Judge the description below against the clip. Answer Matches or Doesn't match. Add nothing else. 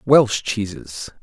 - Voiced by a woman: Doesn't match